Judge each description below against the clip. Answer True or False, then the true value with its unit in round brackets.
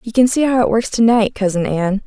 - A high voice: True (220 Hz)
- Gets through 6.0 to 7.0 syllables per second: False (5.6 syllables/s)